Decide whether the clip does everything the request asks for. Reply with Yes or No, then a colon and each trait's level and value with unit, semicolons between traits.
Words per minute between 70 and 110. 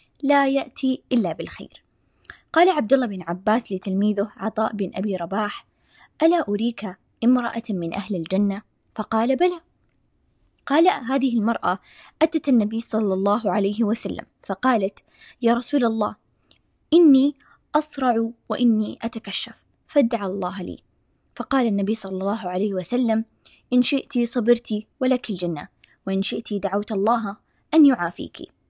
No: average, 125 wpm